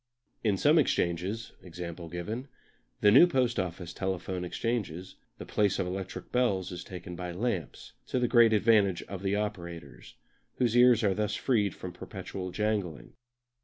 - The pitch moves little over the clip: No, average, 4.3 semitones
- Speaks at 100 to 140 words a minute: No, average, 150 wpm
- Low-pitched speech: Yes, very low, 95 Hz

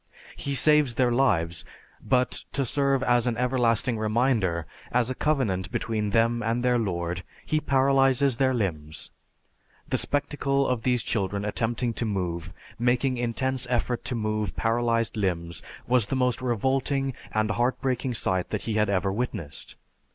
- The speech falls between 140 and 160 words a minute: Yes, average, 150 wpm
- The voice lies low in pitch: Yes, low, 120 Hz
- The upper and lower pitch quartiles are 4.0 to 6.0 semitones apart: No, average, 3.6 semitones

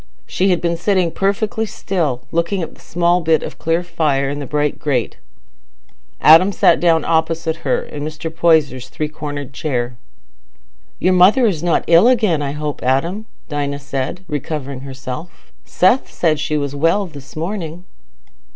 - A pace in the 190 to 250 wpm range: No, average, 160 wpm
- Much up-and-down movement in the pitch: No, average, 3.5 semitones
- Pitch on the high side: No, medium, 160 Hz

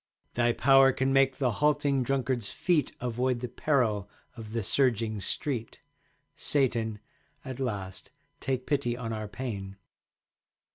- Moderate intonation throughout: Yes, average, 3.2 semitones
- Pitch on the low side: Yes, low, 125 Hz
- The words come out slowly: Yes, slow, 130 wpm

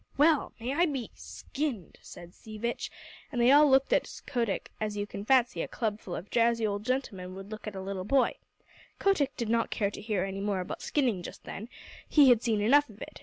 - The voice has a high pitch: Yes, high, 225 Hz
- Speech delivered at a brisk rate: Yes, fast, 220 wpm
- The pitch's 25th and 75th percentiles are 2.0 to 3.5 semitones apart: No, average, 4.8 semitones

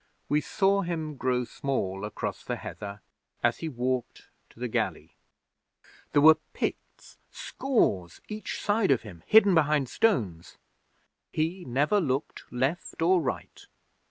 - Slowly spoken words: Yes, slow, 130 wpm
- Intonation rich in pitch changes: Yes, wide, 6.4 semitones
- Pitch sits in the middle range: Yes, medium, 145 Hz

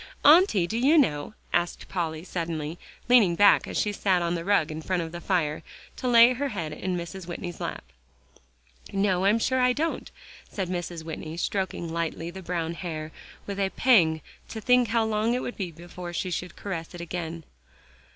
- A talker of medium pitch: Yes, medium, 180 Hz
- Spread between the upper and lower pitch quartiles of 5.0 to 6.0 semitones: No, average, 4.1 semitones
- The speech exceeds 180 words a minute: Yes, average, 190 wpm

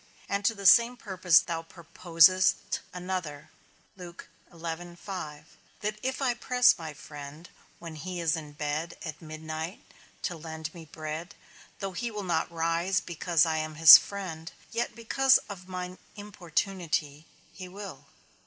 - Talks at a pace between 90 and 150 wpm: Yes, slow, 135 wpm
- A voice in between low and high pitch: Yes, medium, 170 Hz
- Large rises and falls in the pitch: No, average, 3.3 semitones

